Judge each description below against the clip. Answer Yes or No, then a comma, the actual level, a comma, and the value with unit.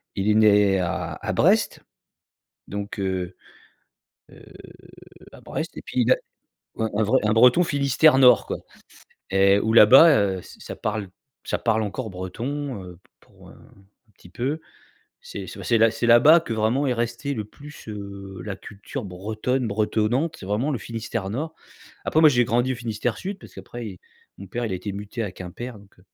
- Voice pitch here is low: Yes, low, 110 Hz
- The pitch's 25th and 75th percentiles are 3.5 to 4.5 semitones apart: Yes, average, 4.2 semitones